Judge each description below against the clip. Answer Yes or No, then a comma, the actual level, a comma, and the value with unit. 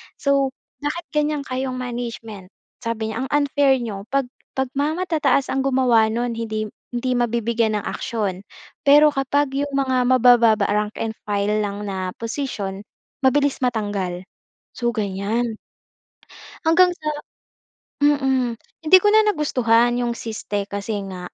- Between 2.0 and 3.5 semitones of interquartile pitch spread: No, average, 4.3 semitones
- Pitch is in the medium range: No, high, 240 Hz